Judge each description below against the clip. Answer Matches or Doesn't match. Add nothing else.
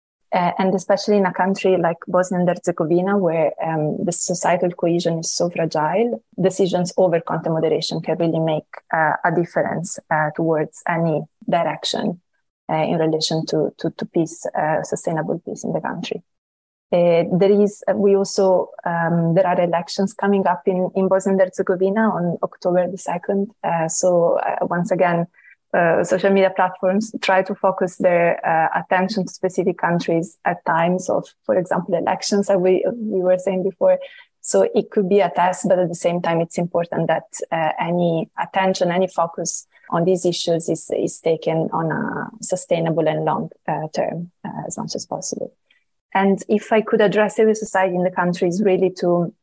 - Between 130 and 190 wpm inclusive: Matches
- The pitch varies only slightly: Matches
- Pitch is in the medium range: Matches